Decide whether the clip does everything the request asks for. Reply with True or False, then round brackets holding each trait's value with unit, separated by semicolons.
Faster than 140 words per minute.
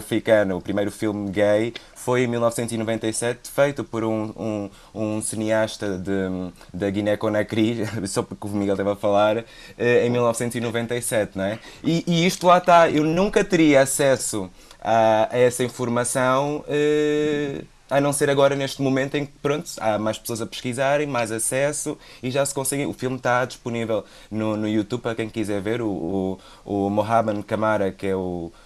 True (170 wpm)